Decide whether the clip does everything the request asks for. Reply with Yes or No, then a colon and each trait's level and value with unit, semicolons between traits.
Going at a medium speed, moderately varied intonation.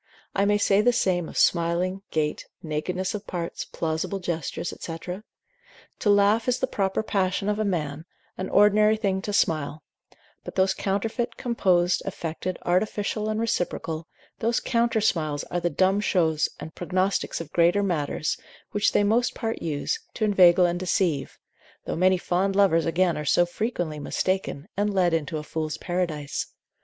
Yes: average, 160 wpm; average, 3.6 semitones